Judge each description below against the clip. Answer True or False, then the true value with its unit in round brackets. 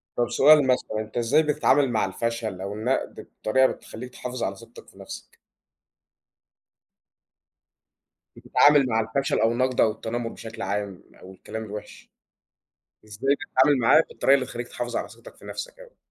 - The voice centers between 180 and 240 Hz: False (120 Hz)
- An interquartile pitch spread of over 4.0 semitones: False (3.5 semitones)